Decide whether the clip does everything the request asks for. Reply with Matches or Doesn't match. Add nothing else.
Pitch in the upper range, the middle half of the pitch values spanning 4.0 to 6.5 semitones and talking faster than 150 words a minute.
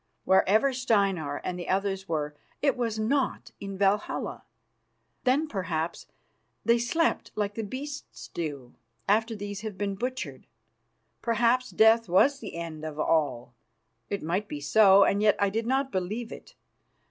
Doesn't match